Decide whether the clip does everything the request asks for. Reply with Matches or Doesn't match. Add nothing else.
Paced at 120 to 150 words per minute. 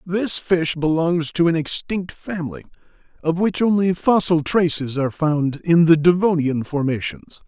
Matches